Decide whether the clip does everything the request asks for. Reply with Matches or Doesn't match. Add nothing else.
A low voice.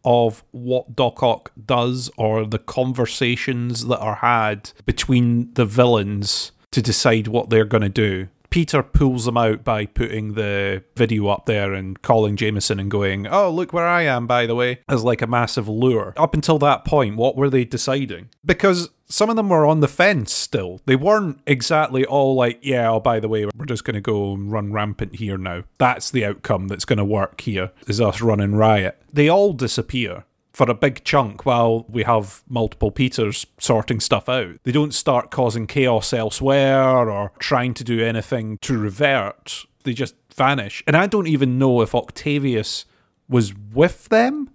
Matches